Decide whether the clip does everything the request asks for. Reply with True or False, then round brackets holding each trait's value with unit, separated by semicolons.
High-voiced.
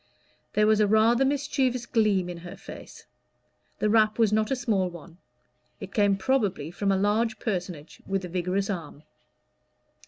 True (205 Hz)